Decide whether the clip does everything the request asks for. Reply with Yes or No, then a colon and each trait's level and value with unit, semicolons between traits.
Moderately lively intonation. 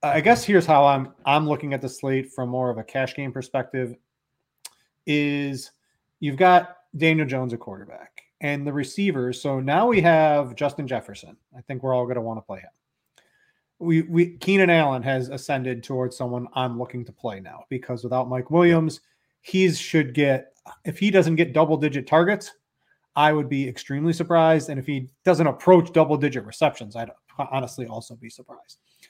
Yes: average, 3.9 semitones